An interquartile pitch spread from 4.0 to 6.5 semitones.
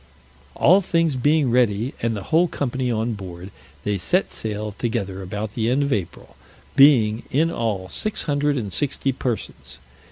Yes: wide, 5.5 semitones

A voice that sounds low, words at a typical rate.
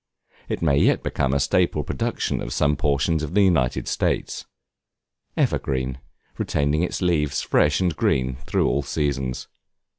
Yes: very low, 70 Hz; average, 145 wpm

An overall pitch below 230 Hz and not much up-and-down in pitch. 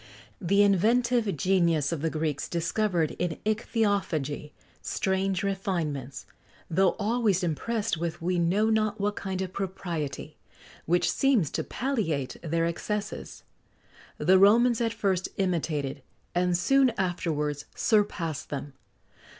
No: medium, 185 Hz; average, 4.3 semitones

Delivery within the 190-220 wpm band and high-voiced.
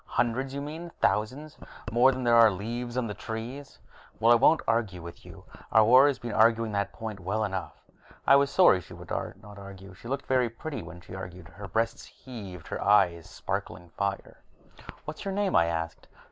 No: average, 195 wpm; low, 110 Hz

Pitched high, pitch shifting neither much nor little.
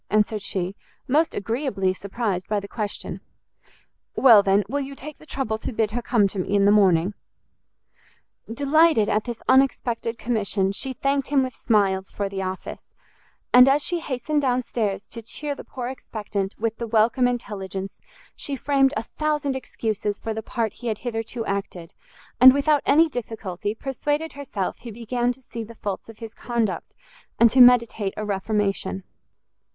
Yes: high, 230 Hz; average, 4.4 semitones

